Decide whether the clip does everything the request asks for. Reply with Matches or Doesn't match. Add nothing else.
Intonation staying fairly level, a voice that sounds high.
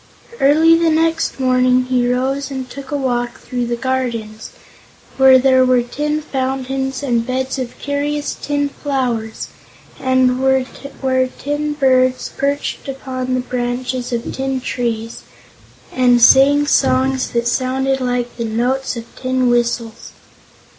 Matches